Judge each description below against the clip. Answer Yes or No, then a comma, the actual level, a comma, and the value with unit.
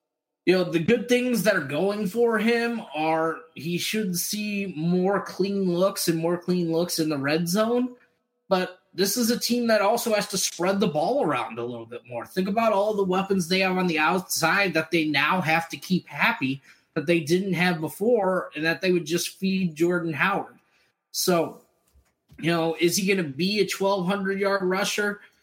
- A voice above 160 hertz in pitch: Yes, medium, 185 Hz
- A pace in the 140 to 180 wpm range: No, average, 200 wpm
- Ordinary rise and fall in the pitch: Yes, average, 3.5 semitones